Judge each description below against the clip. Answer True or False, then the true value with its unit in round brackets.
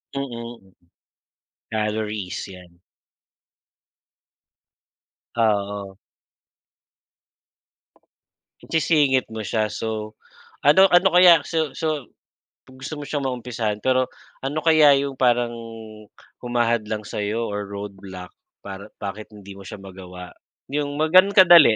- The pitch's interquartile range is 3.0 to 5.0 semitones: False (5.6 semitones)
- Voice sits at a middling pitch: False (115 Hz)